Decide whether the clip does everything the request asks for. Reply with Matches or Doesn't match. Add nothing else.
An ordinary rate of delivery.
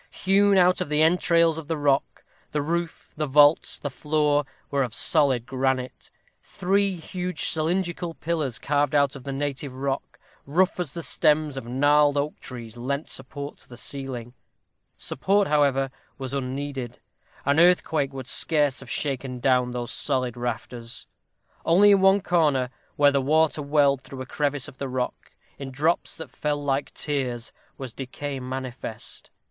Matches